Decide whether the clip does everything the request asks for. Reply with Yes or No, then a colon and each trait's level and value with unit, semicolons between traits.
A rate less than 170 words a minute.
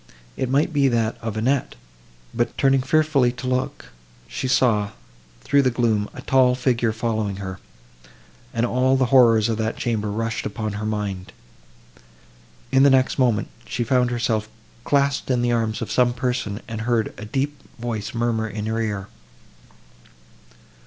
Yes: average, 160 wpm